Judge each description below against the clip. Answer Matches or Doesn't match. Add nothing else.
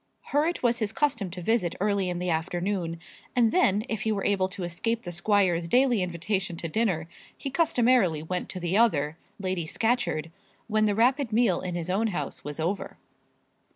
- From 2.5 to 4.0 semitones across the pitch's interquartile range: Doesn't match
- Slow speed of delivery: Doesn't match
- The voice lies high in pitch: Matches